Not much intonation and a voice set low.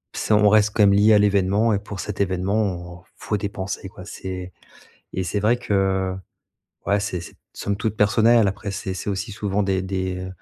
Yes: narrow, 1.8 semitones; low, 100 Hz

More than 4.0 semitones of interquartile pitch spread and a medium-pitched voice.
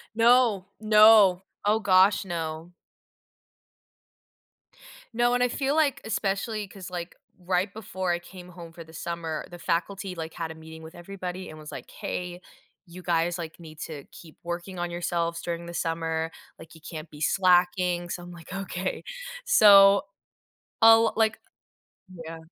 No: average, 2.9 semitones; medium, 180 Hz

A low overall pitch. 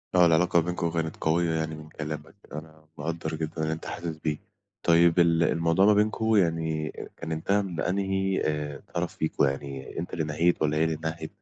Yes: very low, 80 Hz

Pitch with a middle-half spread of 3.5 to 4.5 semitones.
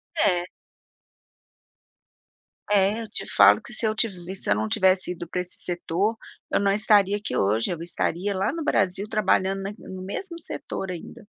No: average, 2.9 semitones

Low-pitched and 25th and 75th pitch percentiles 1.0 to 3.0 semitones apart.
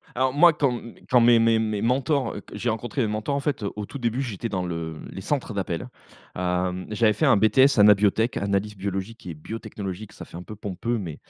No: low, 110 Hz; average, 3.7 semitones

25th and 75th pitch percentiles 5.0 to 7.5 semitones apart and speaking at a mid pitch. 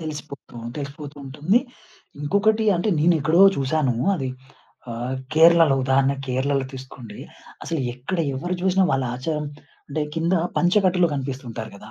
No: average, 4.3 semitones; medium, 145 Hz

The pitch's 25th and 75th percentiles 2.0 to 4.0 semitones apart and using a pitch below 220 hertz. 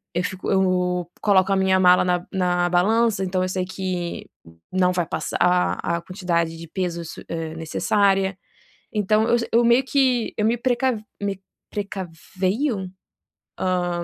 Yes: average, 2.7 semitones; medium, 185 Hz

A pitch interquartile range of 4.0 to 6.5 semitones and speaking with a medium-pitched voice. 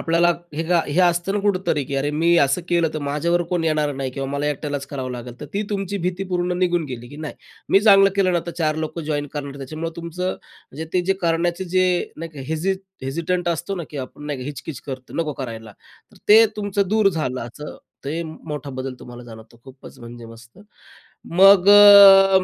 Yes: average, 4.6 semitones; medium, 160 Hz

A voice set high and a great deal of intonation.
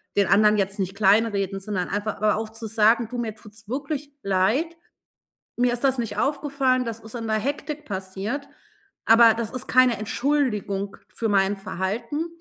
No: high, 225 Hz; average, 3.9 semitones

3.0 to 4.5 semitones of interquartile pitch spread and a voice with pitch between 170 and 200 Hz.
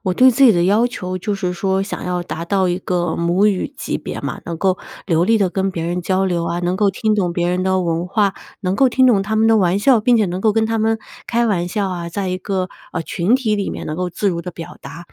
Yes: average, 3.3 semitones; high, 190 Hz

